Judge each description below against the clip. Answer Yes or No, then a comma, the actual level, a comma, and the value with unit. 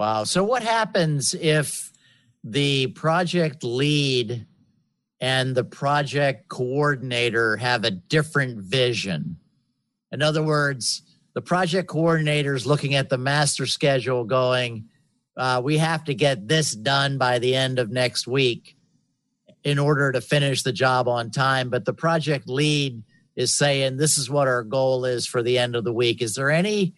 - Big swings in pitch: No, average, 3.1 semitones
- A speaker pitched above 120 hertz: Yes, low, 135 Hz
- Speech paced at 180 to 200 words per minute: No, average, 160 wpm